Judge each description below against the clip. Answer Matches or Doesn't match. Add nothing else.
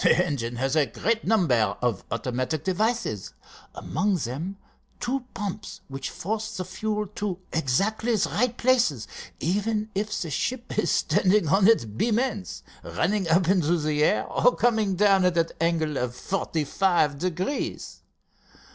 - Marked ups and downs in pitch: Matches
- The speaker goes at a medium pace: Matches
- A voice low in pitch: Doesn't match